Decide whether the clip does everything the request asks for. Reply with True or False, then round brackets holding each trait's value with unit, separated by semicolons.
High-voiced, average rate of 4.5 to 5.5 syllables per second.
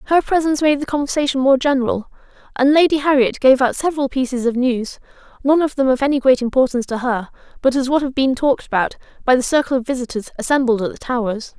False (265 Hz; 6.5 syllables/s)